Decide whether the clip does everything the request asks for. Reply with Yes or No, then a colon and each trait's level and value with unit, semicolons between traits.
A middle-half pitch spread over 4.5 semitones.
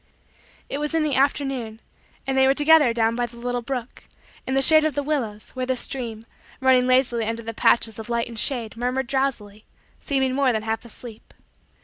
No: average, 2.9 semitones